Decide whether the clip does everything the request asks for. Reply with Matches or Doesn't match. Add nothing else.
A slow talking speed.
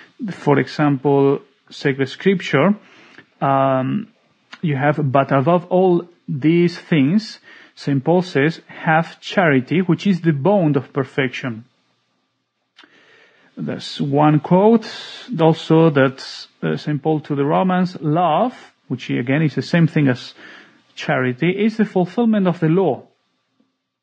Matches